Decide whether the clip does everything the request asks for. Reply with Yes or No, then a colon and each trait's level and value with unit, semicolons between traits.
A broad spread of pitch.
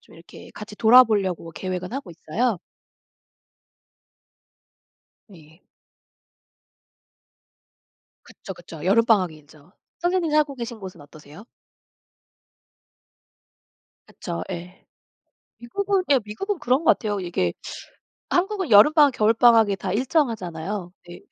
Yes: wide, 6.5 semitones